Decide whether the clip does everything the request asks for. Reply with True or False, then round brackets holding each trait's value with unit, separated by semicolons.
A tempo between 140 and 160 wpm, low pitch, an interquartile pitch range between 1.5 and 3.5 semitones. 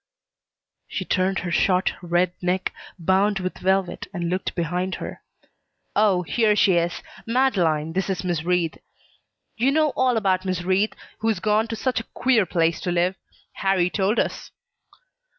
False (155 wpm; 185 Hz; 3.0 semitones)